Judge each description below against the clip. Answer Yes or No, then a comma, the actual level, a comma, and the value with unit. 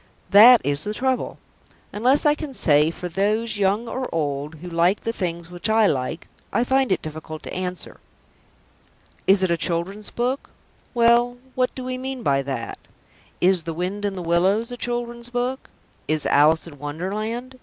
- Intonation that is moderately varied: No, wide, 6.4 semitones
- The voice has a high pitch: Yes, high, 200 Hz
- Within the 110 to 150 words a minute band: No, average, 175 wpm